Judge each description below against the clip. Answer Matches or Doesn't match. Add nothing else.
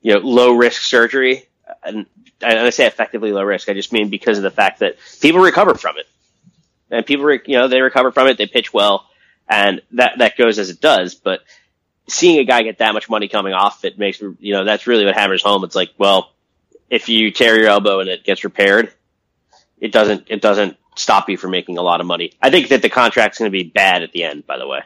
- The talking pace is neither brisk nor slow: Doesn't match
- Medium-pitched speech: Doesn't match